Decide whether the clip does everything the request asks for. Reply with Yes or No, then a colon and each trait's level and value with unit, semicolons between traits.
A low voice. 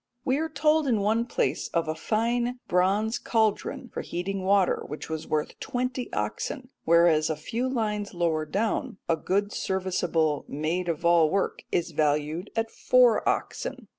No: high, 190 Hz